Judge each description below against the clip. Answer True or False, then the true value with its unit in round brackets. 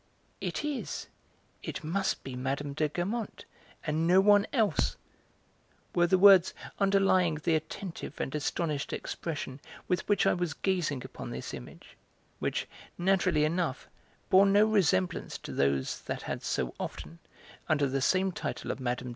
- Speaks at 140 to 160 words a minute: True (145 wpm)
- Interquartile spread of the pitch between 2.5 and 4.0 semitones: False (5.6 semitones)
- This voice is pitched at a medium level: True (170 Hz)